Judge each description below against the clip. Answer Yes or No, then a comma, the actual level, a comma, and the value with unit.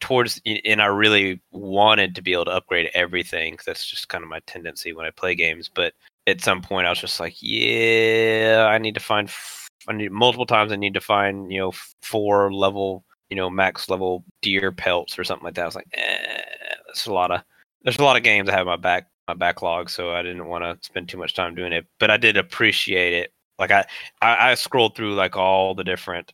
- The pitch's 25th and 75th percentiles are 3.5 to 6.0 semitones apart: No, average, 2.7 semitones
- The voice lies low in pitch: Yes, low, 100 Hz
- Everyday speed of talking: No, fast, 235 wpm